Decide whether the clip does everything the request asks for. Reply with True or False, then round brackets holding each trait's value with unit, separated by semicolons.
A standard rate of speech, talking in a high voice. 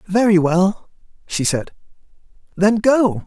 False (110 wpm; 195 Hz)